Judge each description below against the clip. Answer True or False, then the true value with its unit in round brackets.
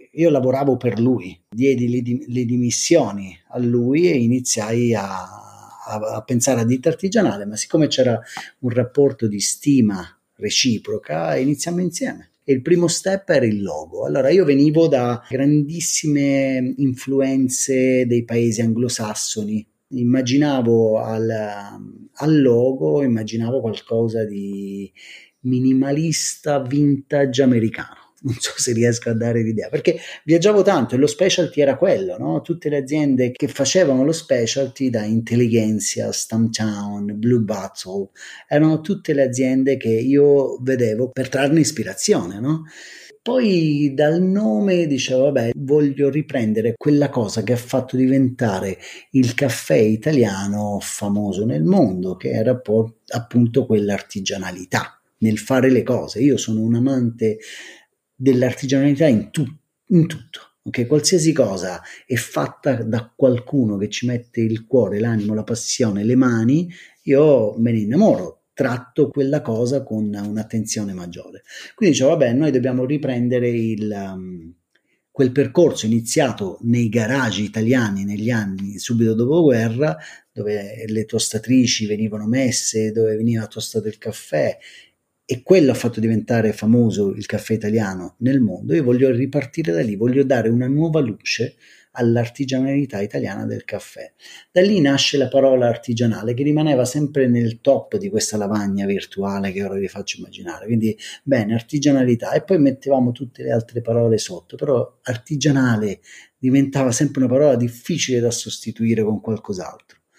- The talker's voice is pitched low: True (125 Hz)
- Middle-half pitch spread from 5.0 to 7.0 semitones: False (4.0 semitones)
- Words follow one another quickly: False (135 wpm)